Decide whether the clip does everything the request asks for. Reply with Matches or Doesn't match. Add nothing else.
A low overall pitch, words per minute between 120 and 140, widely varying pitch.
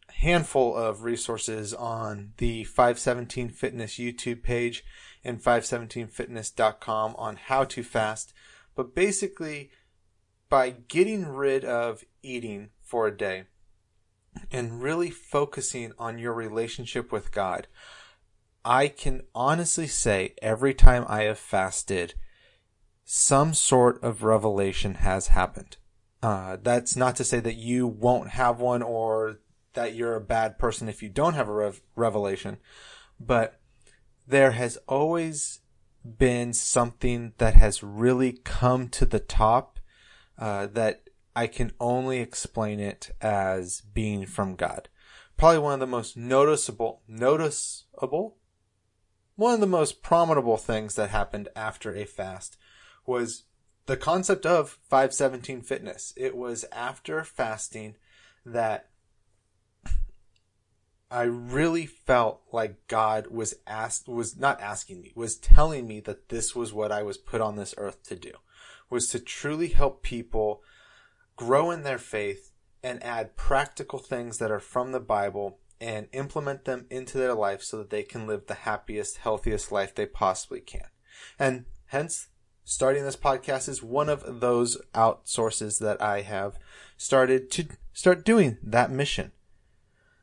Doesn't match